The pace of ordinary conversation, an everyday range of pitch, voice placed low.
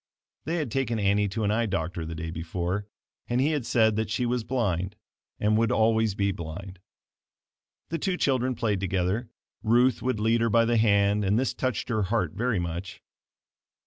Yes: average, 185 wpm; average, 3.8 semitones; low, 110 Hz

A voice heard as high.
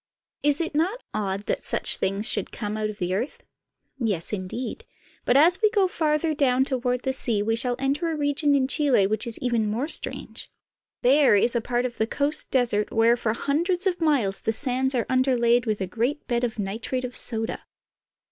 Yes: very high, 250 Hz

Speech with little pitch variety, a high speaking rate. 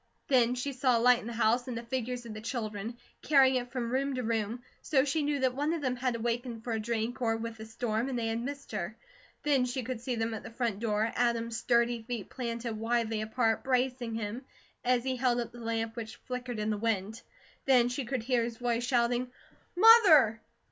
Yes: narrow, 2.0 semitones; fast, 225 wpm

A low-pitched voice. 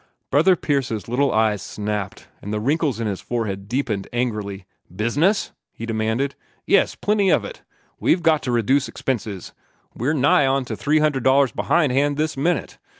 Yes: low, 130 Hz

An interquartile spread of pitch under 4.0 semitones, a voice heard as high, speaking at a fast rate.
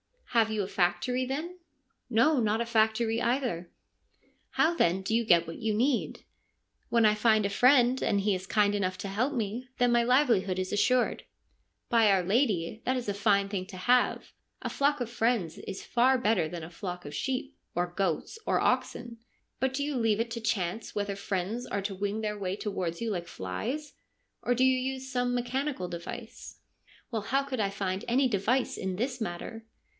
No: average, 4.3 semitones; high, 220 Hz; fast, 210 wpm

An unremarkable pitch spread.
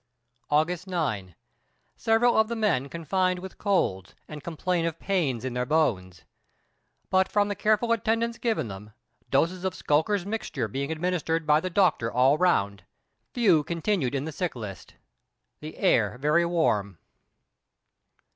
No: wide, 6.5 semitones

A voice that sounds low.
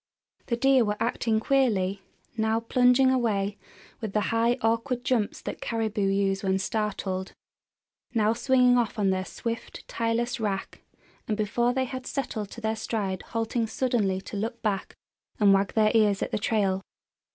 No: high, 220 Hz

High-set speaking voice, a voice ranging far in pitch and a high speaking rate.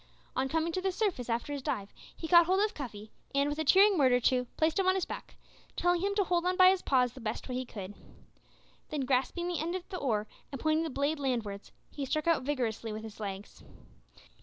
Yes: very high, 285 Hz; wide, 6.0 semitones; fast, 240 wpm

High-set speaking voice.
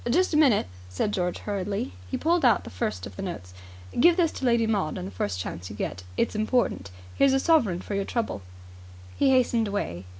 Yes: high, 205 Hz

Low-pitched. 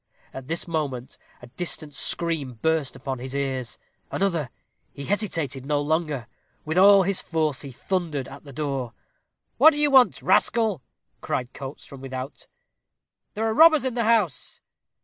No: medium, 150 Hz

